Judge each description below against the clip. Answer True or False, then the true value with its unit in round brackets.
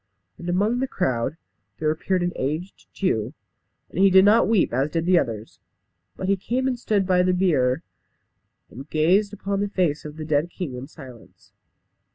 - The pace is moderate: True (185 wpm)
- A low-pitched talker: False (175 Hz)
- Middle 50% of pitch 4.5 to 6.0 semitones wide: True (5.2 semitones)